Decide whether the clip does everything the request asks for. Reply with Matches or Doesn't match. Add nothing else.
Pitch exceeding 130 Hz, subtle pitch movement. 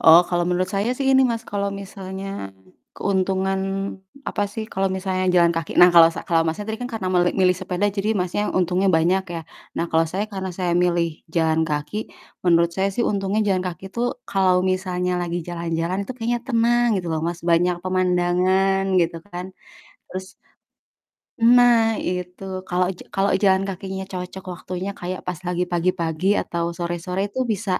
Matches